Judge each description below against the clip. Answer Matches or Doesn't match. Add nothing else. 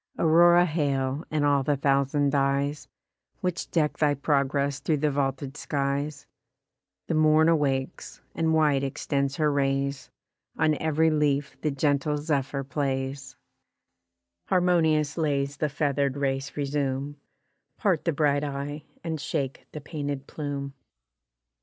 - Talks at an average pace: Doesn't match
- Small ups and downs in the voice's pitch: Matches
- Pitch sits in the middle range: Matches